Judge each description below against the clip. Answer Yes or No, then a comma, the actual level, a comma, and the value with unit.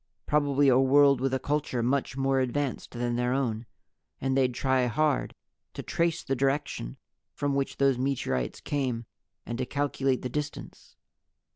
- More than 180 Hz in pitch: No, low, 135 Hz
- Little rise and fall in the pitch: Yes, narrow, 2.2 semitones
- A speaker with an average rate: Yes, average, 155 wpm